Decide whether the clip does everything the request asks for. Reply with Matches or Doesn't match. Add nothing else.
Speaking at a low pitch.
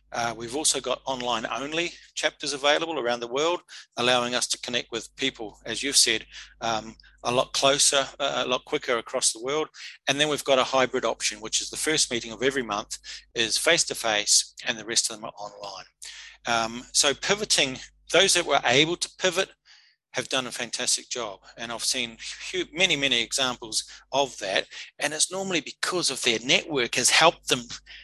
Matches